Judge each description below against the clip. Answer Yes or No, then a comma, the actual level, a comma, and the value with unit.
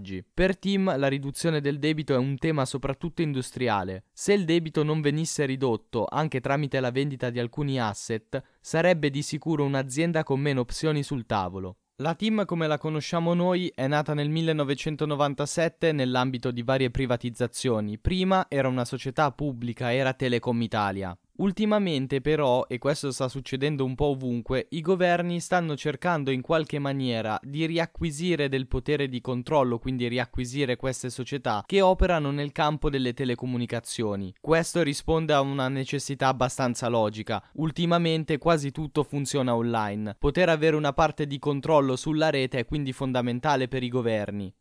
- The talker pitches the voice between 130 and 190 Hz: Yes, medium, 140 Hz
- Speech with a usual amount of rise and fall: Yes, average, 3.8 semitones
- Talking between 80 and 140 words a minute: No, average, 150 wpm